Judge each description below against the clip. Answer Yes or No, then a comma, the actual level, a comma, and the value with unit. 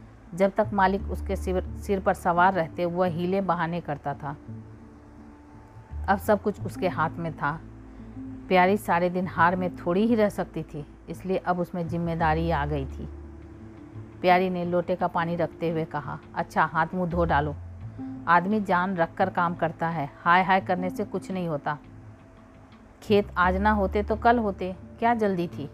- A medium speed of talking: Yes, average, 175 wpm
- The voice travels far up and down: Yes, wide, 6.0 semitones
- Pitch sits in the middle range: Yes, medium, 170 Hz